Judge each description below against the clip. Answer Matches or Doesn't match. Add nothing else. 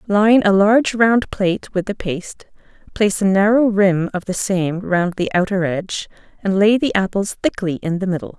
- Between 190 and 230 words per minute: Matches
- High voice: Matches